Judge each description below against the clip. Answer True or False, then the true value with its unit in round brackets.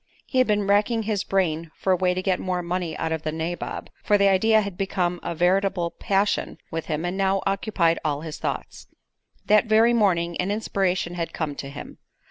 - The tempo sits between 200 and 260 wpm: True (205 wpm)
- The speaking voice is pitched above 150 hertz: True (185 Hz)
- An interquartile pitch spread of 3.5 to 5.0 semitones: False (3.0 semitones)